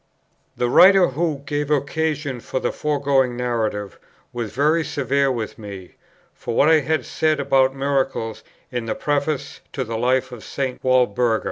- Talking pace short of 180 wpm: Yes, average, 155 wpm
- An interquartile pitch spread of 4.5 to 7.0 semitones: No, average, 3.3 semitones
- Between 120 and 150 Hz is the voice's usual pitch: Yes, low, 135 Hz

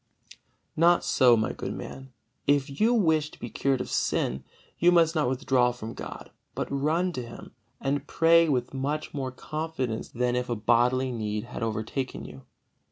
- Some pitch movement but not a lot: Yes, average, 4.1 semitones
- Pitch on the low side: Yes, low, 130 Hz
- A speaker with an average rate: Yes, average, 170 wpm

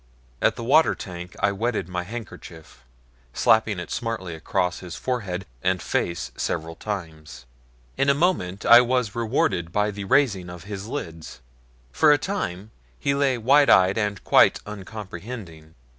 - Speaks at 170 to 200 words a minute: No, average, 150 wpm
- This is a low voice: Yes, low, 100 Hz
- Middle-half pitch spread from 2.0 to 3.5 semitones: No, average, 5.1 semitones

